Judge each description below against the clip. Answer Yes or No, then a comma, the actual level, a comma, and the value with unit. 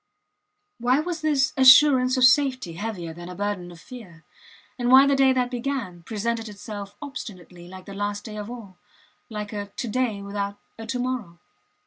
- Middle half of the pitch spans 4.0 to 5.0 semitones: Yes, average, 4.3 semitones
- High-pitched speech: Yes, high, 220 Hz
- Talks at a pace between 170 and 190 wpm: Yes, average, 175 wpm